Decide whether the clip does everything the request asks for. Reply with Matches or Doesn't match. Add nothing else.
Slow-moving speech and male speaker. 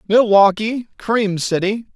Matches